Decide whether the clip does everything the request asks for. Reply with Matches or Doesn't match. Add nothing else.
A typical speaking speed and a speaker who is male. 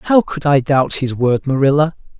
Matches